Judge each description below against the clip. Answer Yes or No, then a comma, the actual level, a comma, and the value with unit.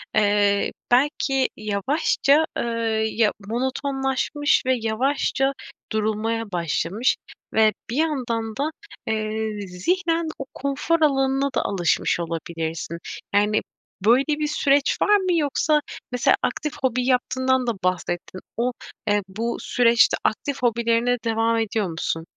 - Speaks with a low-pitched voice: No, high, 235 Hz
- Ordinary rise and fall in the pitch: Yes, average, 4.6 semitones